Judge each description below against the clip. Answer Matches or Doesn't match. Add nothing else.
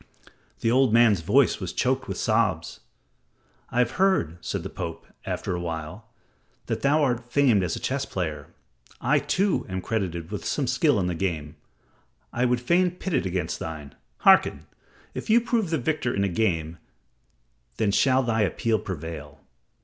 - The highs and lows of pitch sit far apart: Matches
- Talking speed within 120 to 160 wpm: Doesn't match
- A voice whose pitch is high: Doesn't match